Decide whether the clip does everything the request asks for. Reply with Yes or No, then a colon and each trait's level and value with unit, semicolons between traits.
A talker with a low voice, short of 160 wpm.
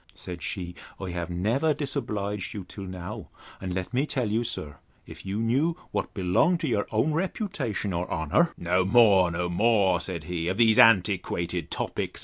No: low, 100 Hz; average, 170 wpm